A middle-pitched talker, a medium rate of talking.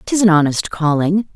Yes: medium, 175 Hz; average, 175 wpm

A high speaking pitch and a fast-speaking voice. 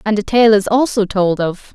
Yes: high, 210 Hz; fast, 240 wpm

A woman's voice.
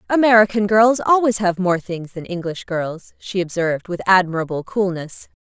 Yes: female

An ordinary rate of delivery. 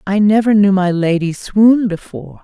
Yes: average, 175 wpm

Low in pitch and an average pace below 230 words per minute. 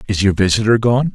Yes: low, 105 Hz; fast, 210 wpm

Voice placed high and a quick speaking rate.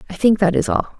Yes: high, 195 Hz; fast, 300 wpm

